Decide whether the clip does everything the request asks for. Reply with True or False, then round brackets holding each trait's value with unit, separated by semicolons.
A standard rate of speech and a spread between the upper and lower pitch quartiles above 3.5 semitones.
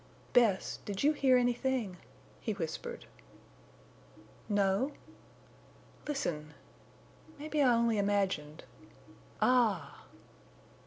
False (70 wpm; 5.4 semitones)